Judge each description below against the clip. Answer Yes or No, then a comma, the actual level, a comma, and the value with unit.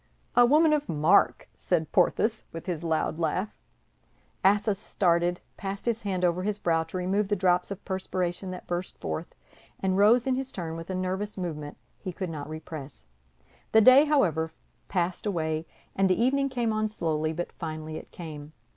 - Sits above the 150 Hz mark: Yes, medium, 185 Hz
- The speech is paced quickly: No, average, 175 wpm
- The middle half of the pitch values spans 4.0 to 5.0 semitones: Yes, average, 4.3 semitones